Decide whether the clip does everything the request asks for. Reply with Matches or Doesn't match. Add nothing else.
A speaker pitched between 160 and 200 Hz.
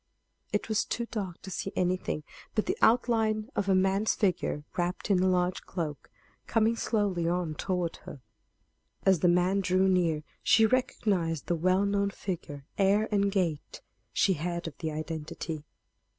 Matches